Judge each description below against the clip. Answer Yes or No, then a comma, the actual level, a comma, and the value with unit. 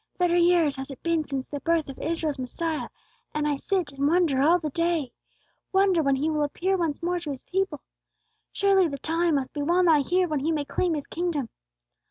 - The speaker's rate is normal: No, fast, 215 wpm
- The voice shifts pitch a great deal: No, average, 3.4 semitones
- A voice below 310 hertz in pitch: No, very high, 320 Hz